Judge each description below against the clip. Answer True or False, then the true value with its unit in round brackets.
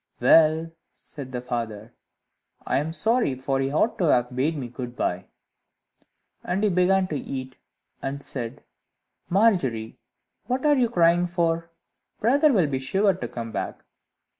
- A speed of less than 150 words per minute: False (155 wpm)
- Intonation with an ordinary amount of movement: False (6.7 semitones)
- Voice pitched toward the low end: False (155 Hz)